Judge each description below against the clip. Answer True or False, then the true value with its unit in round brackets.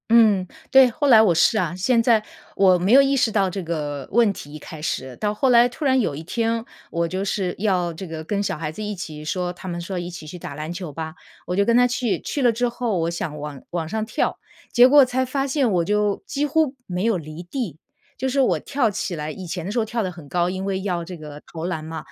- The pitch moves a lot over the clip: True (5.7 semitones)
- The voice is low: False (190 Hz)